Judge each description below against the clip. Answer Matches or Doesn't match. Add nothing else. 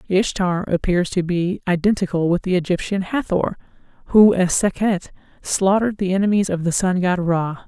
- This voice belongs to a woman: Matches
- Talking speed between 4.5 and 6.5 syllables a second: Matches